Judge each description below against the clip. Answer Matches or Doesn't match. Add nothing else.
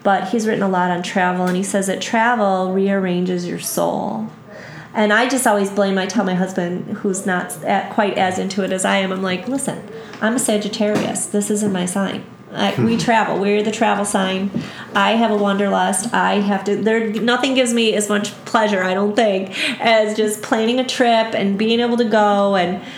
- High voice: Matches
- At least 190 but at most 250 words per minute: Matches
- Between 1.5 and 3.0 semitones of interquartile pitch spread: Matches